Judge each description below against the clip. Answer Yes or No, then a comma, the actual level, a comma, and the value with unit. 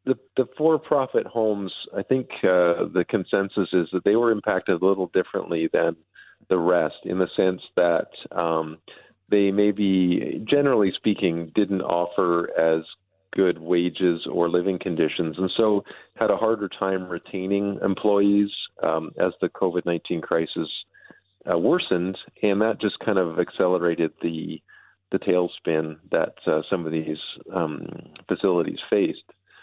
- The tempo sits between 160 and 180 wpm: No, average, 145 wpm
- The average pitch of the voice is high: No, very low, 95 Hz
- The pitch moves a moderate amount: Yes, average, 3.0 semitones